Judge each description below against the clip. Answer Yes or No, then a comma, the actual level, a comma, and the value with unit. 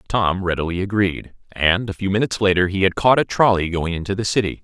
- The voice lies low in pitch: Yes, very low, 95 Hz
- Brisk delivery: Yes, fast, 220 wpm